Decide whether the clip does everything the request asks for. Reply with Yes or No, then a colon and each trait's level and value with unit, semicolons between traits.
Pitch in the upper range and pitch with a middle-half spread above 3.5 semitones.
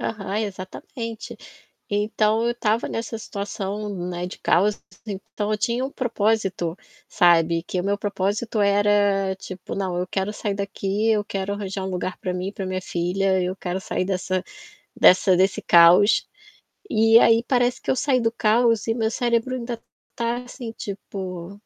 No: high, 205 Hz; average, 3.2 semitones